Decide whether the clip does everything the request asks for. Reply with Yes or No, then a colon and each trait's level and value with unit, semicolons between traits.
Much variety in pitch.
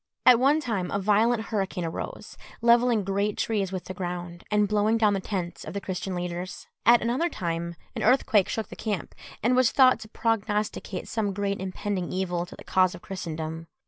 No: average, 3.7 semitones